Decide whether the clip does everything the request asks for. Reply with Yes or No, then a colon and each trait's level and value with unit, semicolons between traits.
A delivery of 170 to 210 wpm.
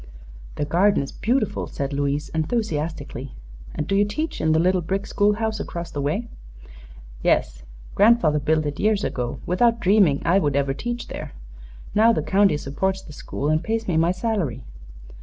Yes: average, 175 wpm